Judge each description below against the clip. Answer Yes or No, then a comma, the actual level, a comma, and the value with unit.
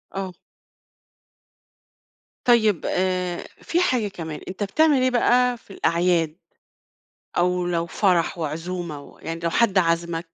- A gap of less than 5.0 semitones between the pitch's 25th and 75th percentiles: Yes, average, 4.1 semitones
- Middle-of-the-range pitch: Yes, medium, 180 Hz